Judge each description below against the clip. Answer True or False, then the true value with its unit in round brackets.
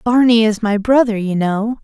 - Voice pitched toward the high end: True (220 Hz)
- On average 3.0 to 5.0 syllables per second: True (4.7 syllables/s)